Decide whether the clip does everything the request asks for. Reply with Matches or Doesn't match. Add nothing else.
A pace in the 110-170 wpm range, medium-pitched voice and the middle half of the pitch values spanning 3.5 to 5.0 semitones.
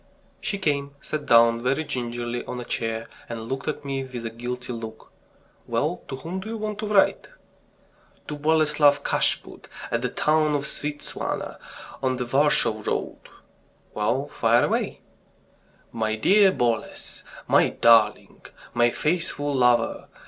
Doesn't match